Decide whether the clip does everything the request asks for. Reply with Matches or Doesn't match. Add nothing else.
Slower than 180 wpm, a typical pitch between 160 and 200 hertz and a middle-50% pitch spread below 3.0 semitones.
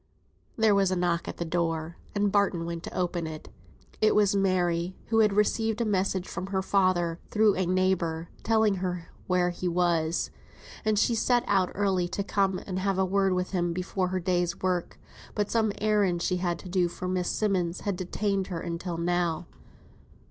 Doesn't match